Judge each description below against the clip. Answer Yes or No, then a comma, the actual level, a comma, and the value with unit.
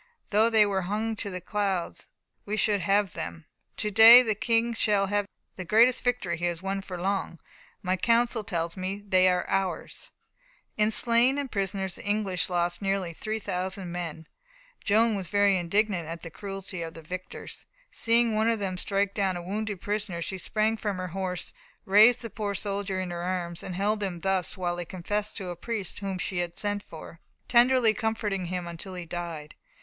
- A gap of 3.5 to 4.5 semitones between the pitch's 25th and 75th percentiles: No, average, 3.1 semitones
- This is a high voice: Yes, high, 195 Hz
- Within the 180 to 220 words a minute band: Yes, average, 190 wpm